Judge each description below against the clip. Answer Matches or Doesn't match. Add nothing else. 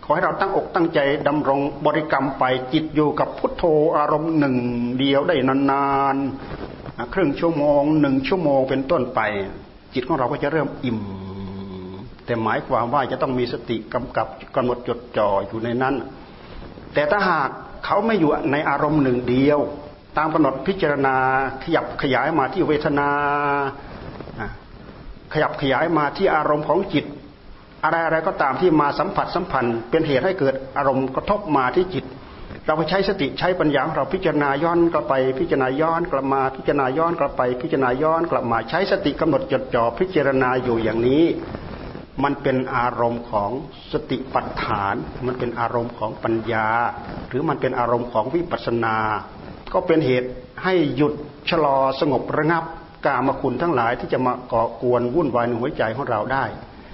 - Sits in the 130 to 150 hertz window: Matches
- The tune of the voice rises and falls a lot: Doesn't match